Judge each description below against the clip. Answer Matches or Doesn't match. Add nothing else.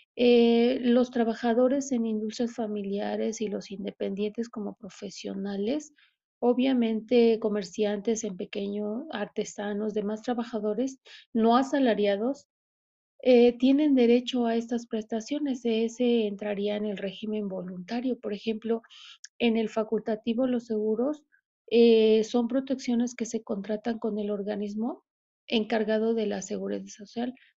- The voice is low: Doesn't match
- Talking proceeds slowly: Matches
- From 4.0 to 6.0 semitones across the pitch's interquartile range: Doesn't match